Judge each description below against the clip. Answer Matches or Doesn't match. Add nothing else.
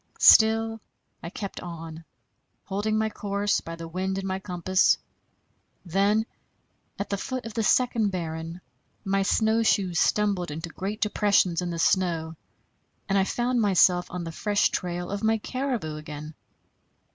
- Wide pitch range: Doesn't match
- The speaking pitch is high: Matches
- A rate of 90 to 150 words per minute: Matches